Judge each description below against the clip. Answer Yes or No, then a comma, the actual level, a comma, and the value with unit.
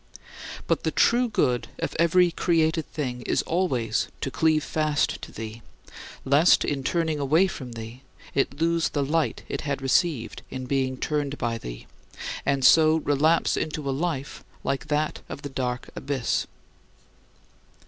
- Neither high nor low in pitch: Yes, medium, 145 Hz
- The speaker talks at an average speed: Yes, average, 150 wpm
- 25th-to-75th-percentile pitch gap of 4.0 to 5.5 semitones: No, average, 3.6 semitones